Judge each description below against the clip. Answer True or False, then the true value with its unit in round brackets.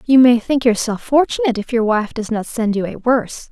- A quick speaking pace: True (240 wpm)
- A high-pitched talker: True (235 Hz)